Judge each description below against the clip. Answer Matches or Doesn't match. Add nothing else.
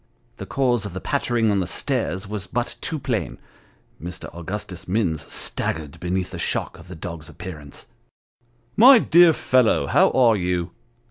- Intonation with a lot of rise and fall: Matches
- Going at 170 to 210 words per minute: Doesn't match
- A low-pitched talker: Matches